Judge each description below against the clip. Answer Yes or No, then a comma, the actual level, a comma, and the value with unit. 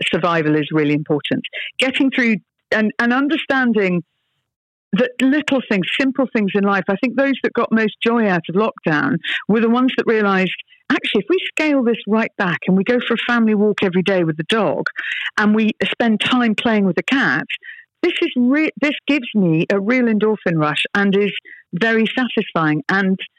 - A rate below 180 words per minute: No, average, 185 wpm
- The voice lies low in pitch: No, high, 220 Hz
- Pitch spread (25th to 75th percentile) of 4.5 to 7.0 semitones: Yes, average, 4.8 semitones